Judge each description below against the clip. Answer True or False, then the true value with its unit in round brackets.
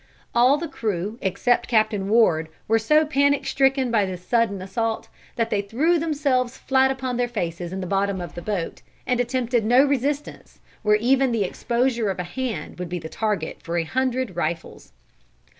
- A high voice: True (230 Hz)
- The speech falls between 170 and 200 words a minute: True (180 wpm)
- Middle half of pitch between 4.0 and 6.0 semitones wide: True (5.3 semitones)